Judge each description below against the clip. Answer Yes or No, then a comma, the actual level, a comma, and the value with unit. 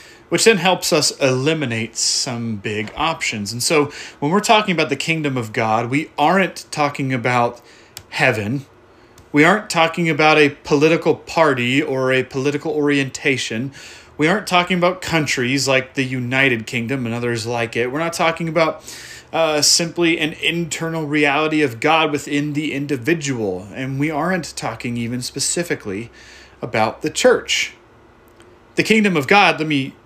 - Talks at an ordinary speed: Yes, average, 150 wpm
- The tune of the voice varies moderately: Yes, average, 4.8 semitones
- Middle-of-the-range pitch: Yes, medium, 145 Hz